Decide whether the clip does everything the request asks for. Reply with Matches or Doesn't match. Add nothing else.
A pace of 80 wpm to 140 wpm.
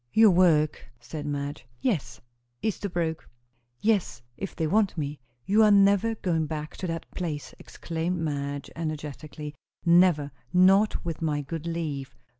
Matches